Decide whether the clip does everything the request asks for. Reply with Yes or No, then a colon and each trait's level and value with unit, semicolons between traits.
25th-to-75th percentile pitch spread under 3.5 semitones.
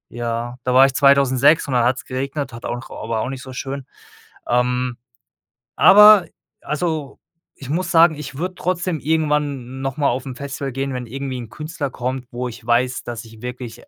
Yes: average, 3.1 semitones